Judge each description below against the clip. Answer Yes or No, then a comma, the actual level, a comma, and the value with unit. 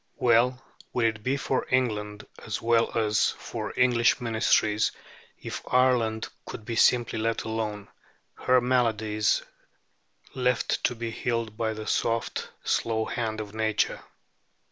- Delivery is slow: Yes, slow, 130 wpm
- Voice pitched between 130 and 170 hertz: No, low, 115 Hz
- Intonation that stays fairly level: Yes, narrow, 2.0 semitones